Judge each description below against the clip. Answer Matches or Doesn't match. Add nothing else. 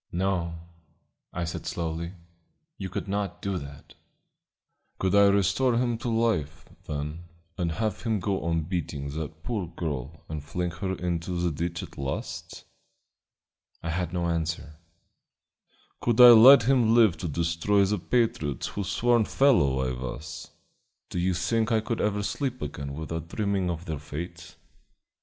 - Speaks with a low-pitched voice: Matches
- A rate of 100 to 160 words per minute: Matches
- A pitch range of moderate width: Matches